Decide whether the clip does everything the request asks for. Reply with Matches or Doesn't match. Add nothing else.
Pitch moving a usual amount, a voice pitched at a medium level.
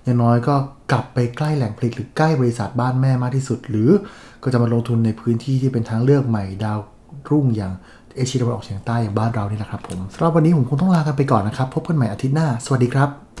Doesn't match